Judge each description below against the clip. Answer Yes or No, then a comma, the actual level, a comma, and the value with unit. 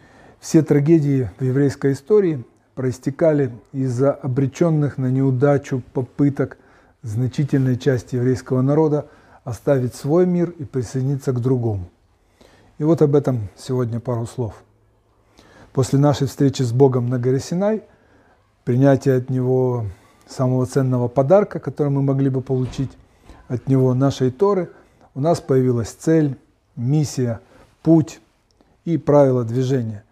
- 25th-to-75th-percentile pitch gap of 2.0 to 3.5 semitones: Yes, narrow, 2.5 semitones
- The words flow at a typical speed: Yes, average, 120 wpm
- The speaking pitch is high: No, low, 130 Hz